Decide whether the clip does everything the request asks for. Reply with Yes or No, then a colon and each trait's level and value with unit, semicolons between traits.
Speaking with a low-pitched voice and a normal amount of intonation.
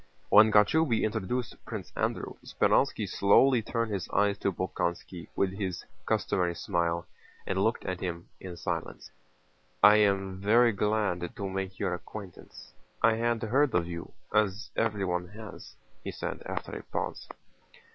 Yes: low, 100 Hz; average, 3.2 semitones